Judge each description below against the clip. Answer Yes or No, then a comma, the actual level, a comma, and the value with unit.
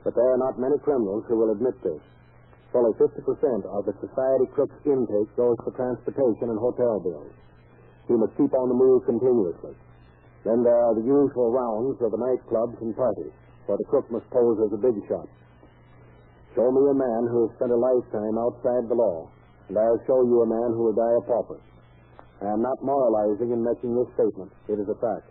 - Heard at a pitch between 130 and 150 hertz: No, low, 120 Hz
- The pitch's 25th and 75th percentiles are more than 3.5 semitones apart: No, average, 2.8 semitones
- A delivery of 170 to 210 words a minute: Yes, average, 200 wpm